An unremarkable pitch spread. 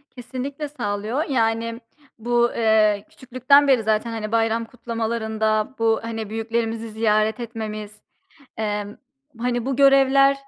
No: narrow, 2.3 semitones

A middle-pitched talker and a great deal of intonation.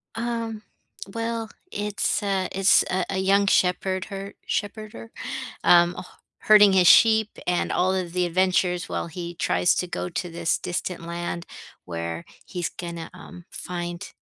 No: medium, 180 Hz; average, 2.7 semitones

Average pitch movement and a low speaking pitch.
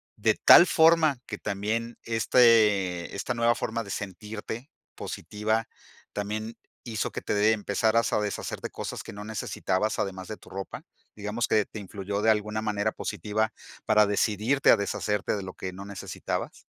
No: narrow, 1.8 semitones; low, 105 Hz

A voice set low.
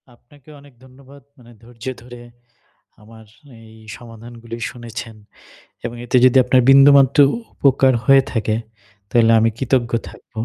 Yes: low, 120 Hz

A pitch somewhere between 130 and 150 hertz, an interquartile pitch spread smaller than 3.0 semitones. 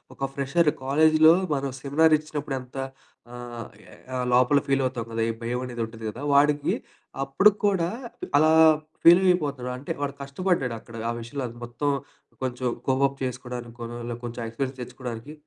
No: low, 135 Hz; average, 3.3 semitones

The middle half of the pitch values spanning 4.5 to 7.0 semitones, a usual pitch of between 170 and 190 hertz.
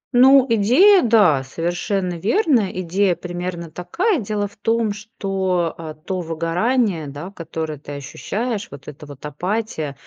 Yes: average, 5.3 semitones; medium, 185 Hz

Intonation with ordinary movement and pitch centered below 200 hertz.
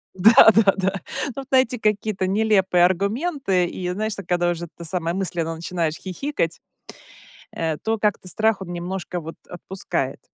Yes: average, 3.7 semitones; high, 190 Hz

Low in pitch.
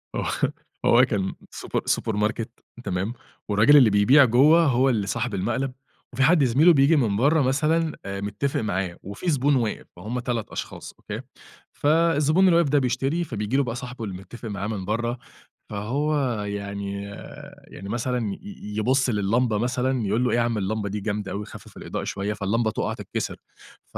Yes: low, 120 Hz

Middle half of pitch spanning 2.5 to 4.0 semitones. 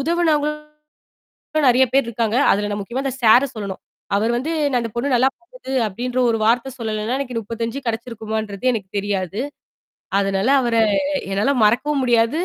Yes: average, 3.6 semitones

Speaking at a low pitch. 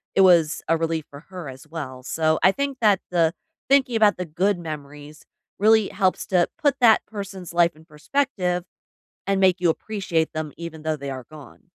No: medium, 170 Hz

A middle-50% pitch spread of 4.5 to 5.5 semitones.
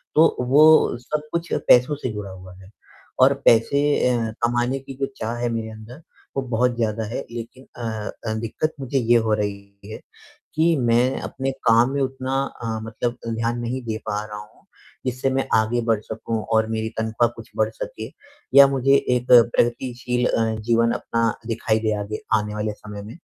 No: average, 2.8 semitones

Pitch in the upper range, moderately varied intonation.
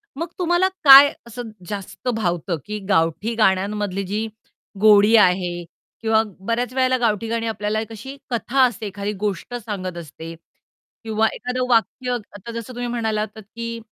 Yes: high, 220 Hz; average, 3.2 semitones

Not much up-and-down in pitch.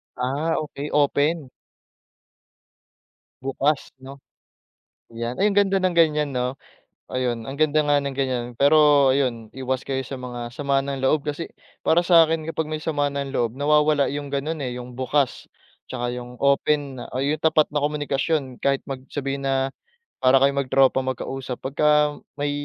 Yes: narrow, 2.3 semitones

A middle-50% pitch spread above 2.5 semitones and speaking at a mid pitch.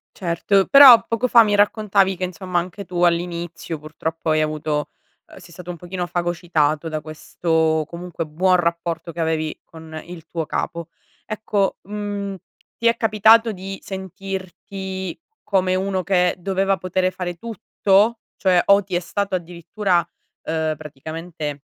Yes: average, 2.9 semitones; medium, 180 Hz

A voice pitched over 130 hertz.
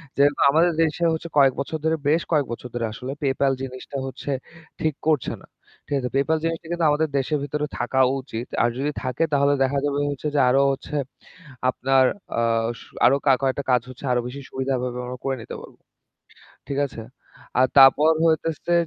Yes: medium, 140 Hz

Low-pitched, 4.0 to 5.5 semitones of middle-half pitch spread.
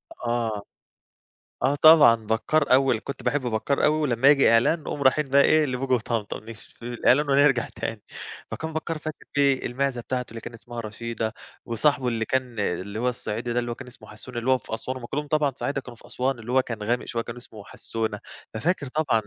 No: low, 125 Hz; average, 3.3 semitones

